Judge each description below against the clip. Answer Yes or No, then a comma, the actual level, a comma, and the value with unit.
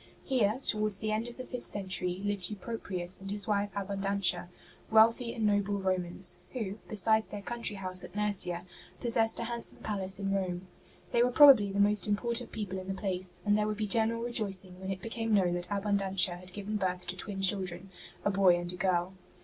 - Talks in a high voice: Yes, high, 200 Hz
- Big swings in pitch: No, narrow, 2.6 semitones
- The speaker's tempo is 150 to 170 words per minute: No, average, 200 wpm